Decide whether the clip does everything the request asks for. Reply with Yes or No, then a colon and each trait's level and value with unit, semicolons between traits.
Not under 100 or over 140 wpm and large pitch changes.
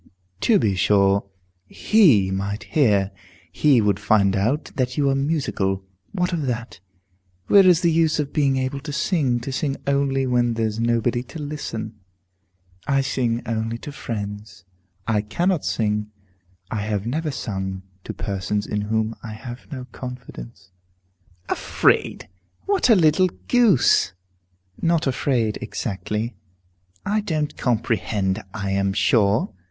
Yes: slow, 135 wpm; wide, 5.7 semitones